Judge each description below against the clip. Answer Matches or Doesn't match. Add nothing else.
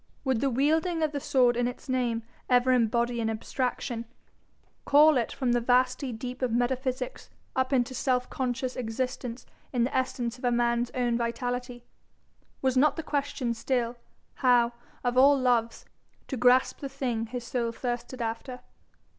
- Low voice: Doesn't match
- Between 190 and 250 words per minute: Doesn't match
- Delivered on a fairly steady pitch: Matches